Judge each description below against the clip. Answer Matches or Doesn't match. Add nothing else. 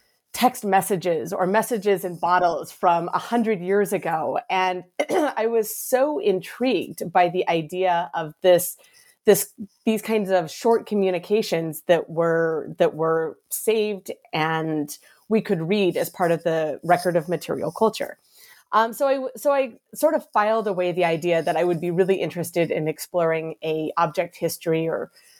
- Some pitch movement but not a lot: Matches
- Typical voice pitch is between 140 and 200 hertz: Matches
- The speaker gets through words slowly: Doesn't match